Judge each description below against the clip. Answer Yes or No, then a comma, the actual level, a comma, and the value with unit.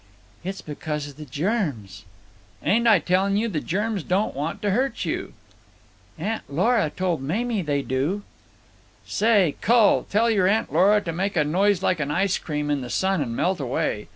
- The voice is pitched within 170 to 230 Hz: Yes, medium, 185 Hz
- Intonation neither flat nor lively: No, wide, 5.7 semitones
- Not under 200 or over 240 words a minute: No, average, 180 wpm